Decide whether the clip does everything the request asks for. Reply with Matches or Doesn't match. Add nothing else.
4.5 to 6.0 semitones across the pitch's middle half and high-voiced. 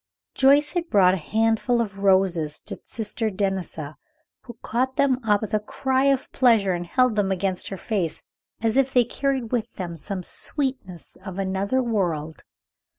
Matches